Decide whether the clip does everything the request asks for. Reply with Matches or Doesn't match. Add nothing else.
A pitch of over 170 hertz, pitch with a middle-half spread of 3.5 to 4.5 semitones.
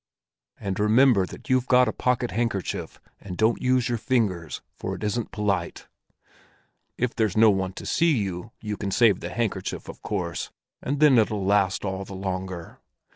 Doesn't match